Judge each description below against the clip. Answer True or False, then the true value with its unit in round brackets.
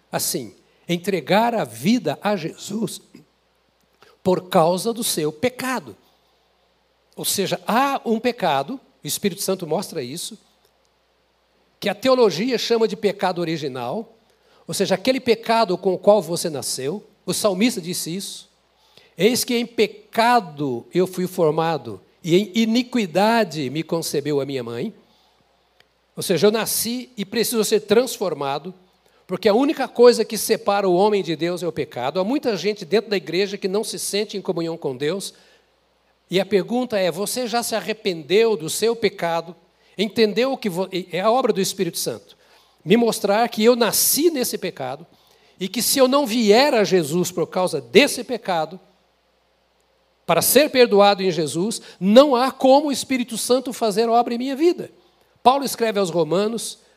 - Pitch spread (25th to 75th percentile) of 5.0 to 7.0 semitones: False (4.2 semitones)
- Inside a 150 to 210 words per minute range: True (160 wpm)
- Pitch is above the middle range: True (205 Hz)